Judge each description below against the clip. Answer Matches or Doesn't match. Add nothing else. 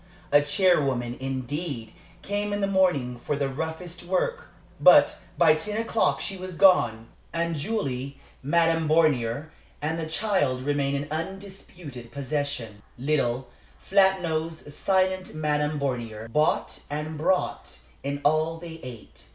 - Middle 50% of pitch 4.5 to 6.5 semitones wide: Matches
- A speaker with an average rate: Doesn't match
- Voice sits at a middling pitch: Matches